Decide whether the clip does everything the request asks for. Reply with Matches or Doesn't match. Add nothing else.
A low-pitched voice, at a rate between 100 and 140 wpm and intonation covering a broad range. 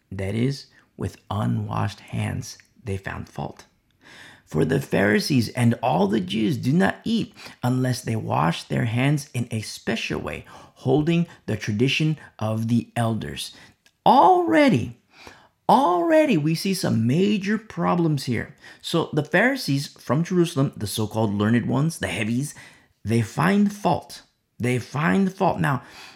Matches